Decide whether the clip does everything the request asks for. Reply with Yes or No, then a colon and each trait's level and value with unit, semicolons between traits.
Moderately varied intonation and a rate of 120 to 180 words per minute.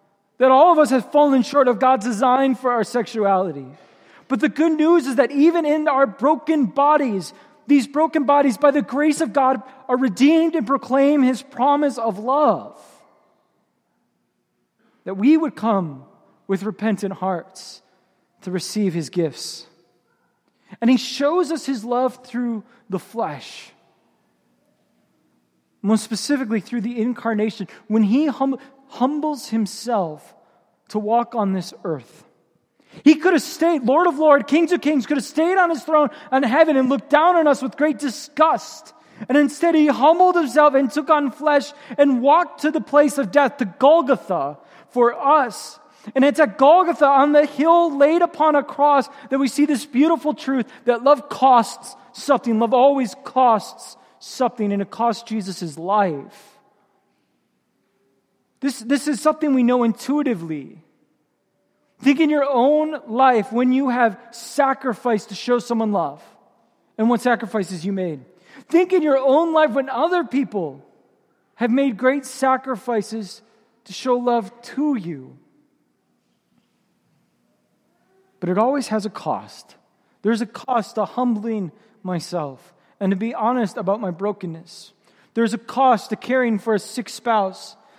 Yes: average, 4.8 semitones; average, 150 wpm